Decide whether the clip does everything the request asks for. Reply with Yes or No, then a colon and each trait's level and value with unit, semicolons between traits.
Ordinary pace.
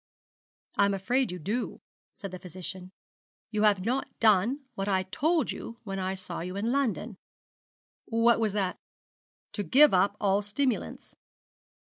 Yes: average, 145 wpm